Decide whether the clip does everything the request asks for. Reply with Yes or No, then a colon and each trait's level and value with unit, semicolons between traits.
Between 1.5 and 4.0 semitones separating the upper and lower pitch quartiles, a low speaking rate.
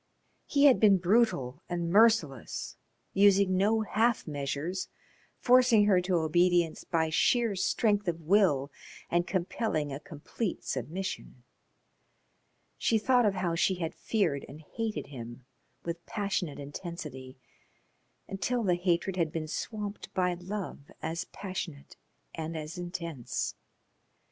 No: average, 4.5 semitones; slow, 125 wpm